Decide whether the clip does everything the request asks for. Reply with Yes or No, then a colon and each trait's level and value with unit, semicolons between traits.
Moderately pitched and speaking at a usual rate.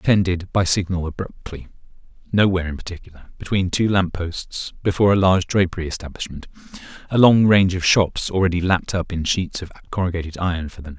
No: very low, 90 Hz; average, 175 wpm